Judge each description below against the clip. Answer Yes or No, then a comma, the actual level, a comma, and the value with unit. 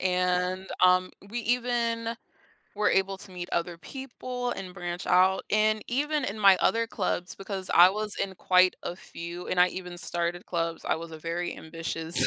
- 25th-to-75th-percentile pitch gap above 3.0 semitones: Yes, average, 3.5 semitones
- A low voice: No, medium, 185 Hz